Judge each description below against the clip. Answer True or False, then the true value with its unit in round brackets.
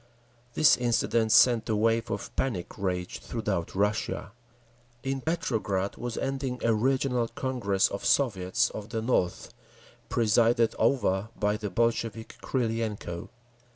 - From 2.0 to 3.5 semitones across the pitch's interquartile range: True (3.0 semitones)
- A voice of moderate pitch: False (115 Hz)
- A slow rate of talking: True (120 wpm)